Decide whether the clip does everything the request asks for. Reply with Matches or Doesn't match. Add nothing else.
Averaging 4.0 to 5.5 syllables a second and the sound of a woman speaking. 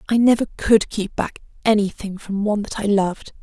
Matches